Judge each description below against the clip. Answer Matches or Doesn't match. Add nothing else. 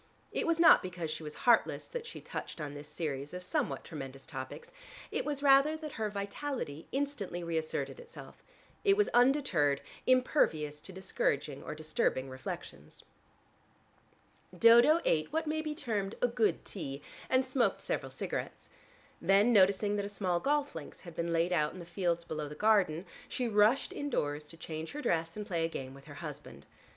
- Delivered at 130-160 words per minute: Doesn't match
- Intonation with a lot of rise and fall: Matches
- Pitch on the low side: Doesn't match